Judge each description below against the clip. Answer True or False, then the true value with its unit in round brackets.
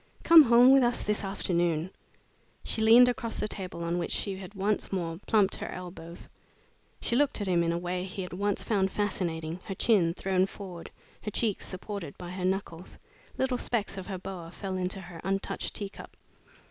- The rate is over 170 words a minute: True (185 wpm)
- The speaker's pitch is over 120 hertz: True (190 Hz)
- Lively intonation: False (3.0 semitones)